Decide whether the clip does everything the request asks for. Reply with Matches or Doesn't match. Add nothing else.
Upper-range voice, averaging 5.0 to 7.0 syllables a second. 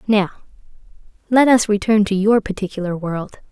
Matches